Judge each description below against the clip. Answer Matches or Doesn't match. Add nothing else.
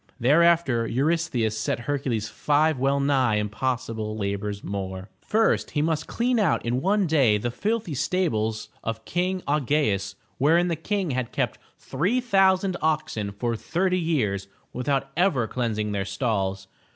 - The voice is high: Doesn't match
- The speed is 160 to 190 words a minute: Doesn't match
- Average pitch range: Doesn't match